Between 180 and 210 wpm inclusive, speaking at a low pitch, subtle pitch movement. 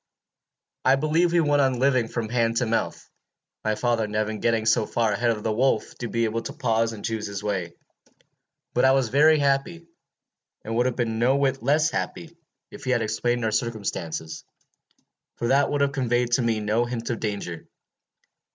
No: average, 195 wpm; low, 120 Hz; average, 3.5 semitones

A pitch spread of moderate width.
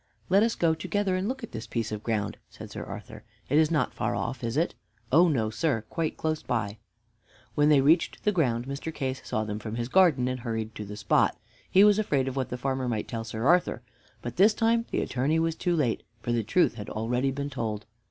No: wide, 6.3 semitones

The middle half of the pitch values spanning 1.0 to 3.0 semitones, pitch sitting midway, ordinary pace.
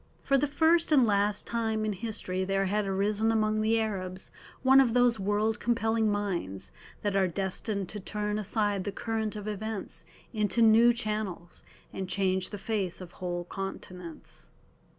No: narrow, 2.6 semitones; high, 210 Hz; average, 160 wpm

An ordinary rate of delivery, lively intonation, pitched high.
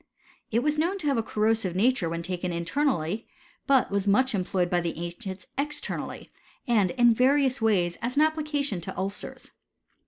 Yes: average, 180 wpm; wide, 7.1 semitones; high, 220 Hz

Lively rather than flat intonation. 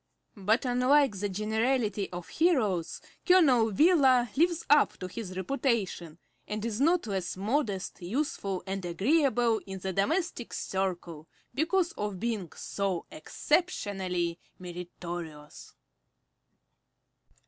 Yes: wide, 6.8 semitones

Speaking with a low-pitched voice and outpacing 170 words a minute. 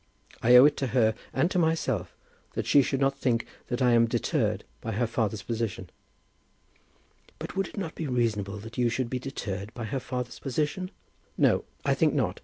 Yes: low, 125 Hz; average, 195 wpm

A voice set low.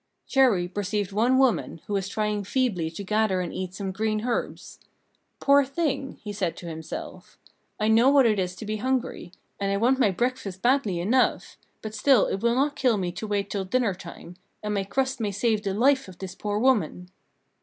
No: high, 210 Hz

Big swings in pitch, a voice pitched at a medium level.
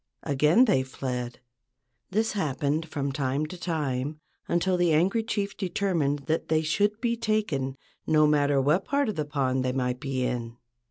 Yes: wide, 5.7 semitones; medium, 150 Hz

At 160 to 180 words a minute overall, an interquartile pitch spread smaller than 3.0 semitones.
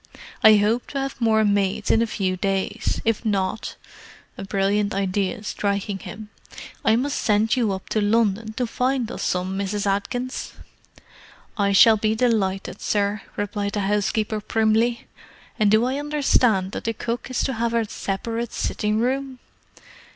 No: average, 150 wpm; narrow, 2.5 semitones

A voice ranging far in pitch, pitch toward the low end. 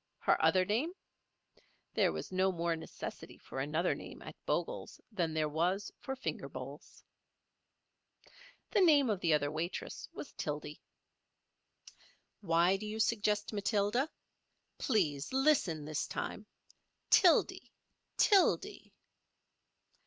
No: wide, 5.9 semitones; high, 195 Hz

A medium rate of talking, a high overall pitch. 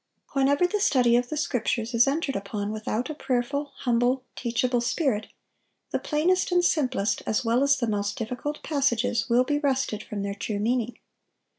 Yes: average, 170 wpm; very high, 250 Hz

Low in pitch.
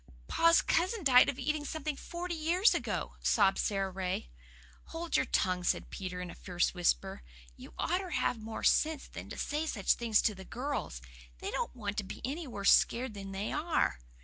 No: high, 240 Hz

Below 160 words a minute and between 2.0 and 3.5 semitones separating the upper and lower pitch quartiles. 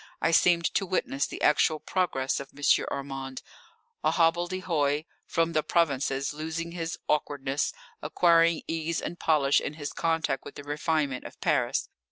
Yes: average, 150 wpm; average, 2.9 semitones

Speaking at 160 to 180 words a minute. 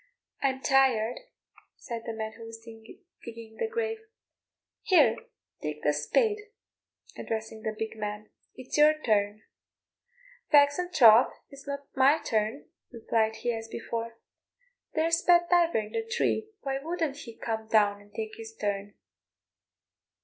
No: average, 140 wpm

